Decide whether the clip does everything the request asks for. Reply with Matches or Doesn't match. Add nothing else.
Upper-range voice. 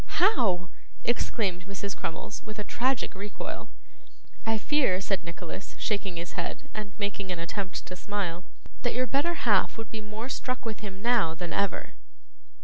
Matches